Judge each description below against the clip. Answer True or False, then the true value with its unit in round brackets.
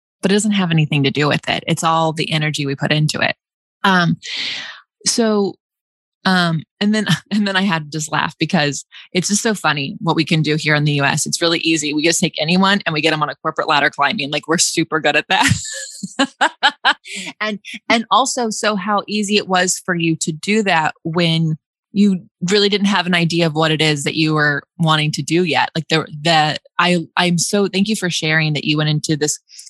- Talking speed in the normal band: False (220 wpm)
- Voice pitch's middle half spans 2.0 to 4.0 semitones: False (4.5 semitones)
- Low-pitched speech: False (170 Hz)